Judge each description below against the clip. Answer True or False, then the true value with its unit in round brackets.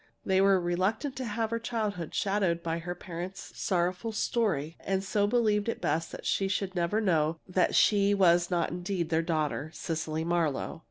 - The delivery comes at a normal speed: True (175 wpm)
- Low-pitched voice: False (185 Hz)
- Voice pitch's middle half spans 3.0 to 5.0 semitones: True (3.3 semitones)